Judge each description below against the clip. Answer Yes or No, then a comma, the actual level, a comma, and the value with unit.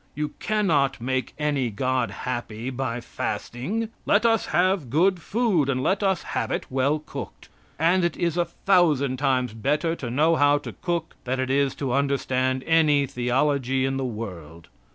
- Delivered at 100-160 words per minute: No, average, 175 wpm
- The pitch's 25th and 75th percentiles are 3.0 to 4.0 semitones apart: No, average, 4.5 semitones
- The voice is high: No, medium, 140 Hz